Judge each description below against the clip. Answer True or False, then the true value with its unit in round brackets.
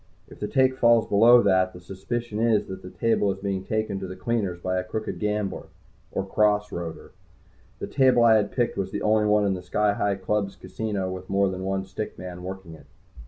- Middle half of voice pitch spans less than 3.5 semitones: True (2.5 semitones)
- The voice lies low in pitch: True (100 Hz)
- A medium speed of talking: False (215 wpm)